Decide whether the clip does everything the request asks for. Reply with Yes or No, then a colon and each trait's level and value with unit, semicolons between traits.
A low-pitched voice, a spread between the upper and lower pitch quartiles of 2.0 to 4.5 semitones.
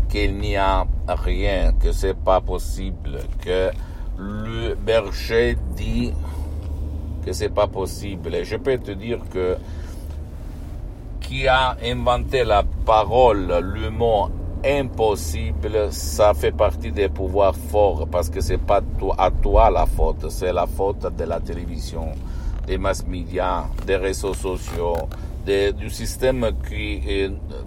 Yes: very low, 90 Hz; average, 4.2 semitones